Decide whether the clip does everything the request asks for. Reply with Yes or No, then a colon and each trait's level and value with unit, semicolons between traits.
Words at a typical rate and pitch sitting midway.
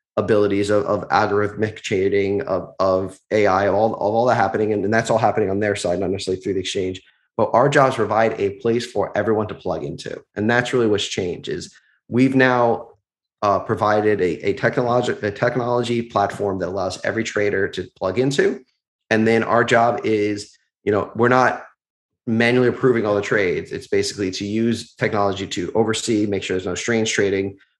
No: average, 190 wpm; low, 105 Hz